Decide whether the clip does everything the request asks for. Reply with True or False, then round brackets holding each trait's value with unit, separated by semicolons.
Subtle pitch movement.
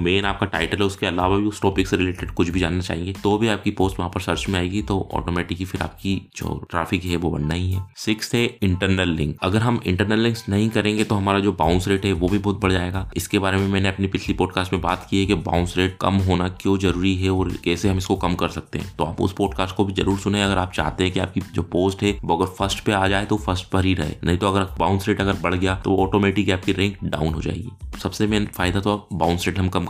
True (2.0 semitones)